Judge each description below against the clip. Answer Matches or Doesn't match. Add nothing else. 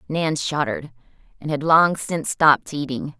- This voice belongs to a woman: Matches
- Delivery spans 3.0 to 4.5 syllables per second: Doesn't match